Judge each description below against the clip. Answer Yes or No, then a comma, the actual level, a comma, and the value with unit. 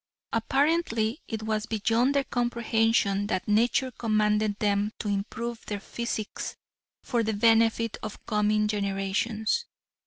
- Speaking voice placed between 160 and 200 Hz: No, high, 220 Hz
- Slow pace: Yes, slow, 120 wpm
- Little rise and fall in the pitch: Yes, narrow, 1.8 semitones